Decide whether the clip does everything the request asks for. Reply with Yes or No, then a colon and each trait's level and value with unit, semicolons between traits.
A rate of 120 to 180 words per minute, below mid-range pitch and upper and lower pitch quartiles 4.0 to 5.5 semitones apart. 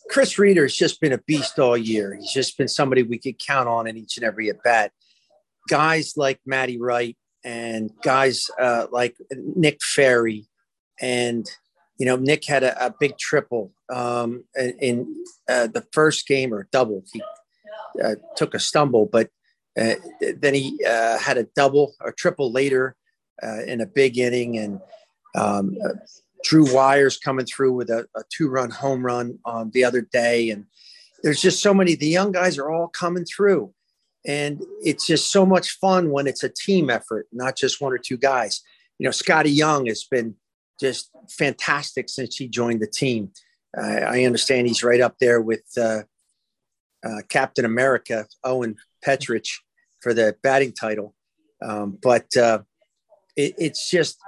Yes: average, 170 wpm; low, 130 Hz; average, 4.7 semitones